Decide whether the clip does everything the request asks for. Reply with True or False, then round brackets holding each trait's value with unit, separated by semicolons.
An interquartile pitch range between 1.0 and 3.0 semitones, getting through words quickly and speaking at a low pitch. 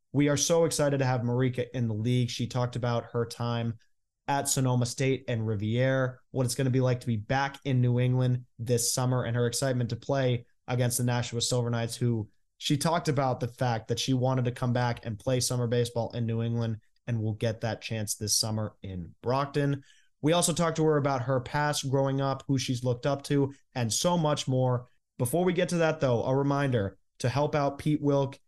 True (2.7 semitones; 220 wpm; 125 Hz)